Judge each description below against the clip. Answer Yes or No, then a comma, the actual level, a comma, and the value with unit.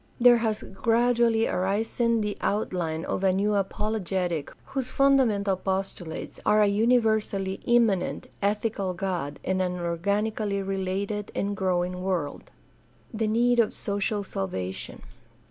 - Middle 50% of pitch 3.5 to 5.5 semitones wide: No, average, 3.0 semitones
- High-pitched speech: Yes, high, 200 Hz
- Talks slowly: Yes, slow, 125 wpm